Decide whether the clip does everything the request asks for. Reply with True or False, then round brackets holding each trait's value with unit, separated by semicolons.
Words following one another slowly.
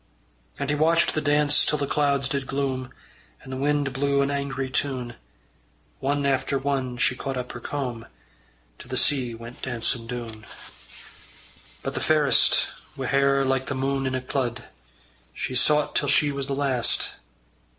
False (165 wpm)